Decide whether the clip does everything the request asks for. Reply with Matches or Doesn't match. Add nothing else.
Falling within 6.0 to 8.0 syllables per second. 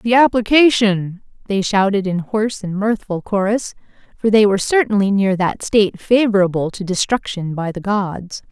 Doesn't match